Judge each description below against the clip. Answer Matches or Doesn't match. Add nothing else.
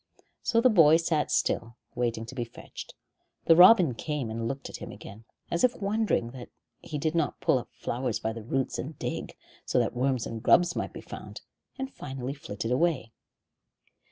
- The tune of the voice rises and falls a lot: Matches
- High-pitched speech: Doesn't match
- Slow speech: Doesn't match